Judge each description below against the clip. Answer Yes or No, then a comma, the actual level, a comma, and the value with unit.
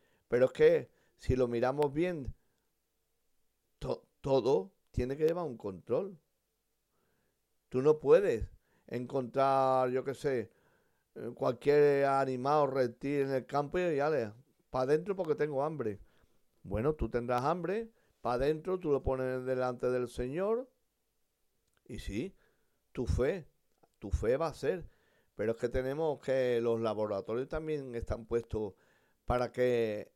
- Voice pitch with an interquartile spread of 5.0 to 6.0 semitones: No, average, 4.1 semitones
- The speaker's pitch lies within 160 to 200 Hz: No, low, 135 Hz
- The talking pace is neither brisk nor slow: Yes, average, 135 wpm